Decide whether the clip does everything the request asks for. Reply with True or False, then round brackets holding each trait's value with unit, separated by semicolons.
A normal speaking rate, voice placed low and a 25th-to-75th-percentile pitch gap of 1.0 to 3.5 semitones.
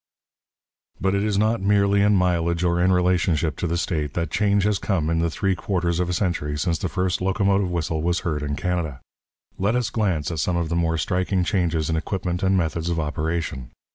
False (210 wpm; 90 Hz; 2.8 semitones)